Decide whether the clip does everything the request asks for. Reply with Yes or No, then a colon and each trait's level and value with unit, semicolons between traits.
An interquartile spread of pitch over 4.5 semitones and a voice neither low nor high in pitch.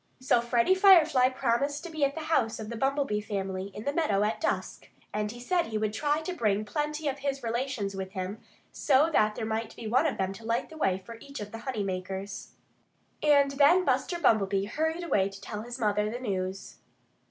No: wide, 5.6 semitones; high, 235 Hz